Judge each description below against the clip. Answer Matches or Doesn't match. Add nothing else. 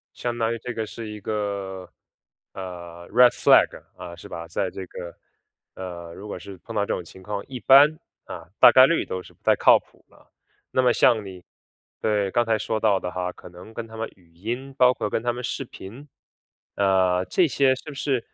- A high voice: Doesn't match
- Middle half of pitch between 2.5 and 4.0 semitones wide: Doesn't match